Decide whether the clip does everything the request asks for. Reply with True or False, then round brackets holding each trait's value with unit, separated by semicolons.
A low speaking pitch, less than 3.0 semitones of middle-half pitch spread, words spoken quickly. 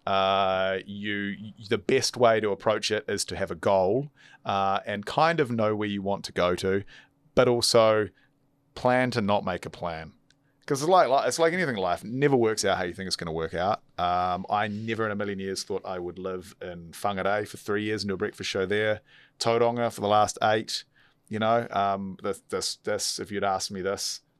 False (105 Hz; 3.4 semitones; 220 wpm)